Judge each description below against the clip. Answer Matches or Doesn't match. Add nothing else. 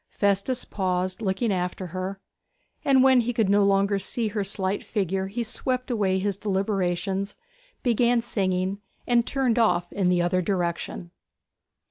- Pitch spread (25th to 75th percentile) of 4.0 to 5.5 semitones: Doesn't match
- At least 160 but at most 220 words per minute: Doesn't match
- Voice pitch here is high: Matches